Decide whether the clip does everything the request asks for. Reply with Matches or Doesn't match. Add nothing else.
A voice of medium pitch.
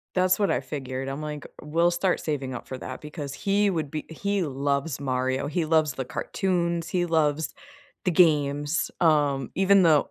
Matches